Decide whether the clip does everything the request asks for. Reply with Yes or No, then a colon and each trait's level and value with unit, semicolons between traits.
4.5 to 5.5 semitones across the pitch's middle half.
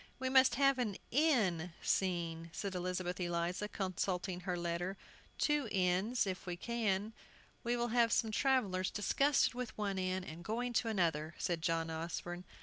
Yes: average, 5.0 semitones